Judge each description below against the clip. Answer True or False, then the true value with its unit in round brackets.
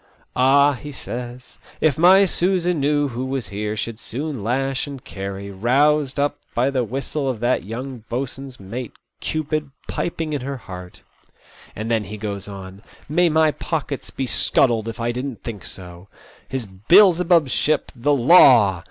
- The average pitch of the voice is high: False (130 Hz)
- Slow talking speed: False (175 wpm)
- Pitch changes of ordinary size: True (4.9 semitones)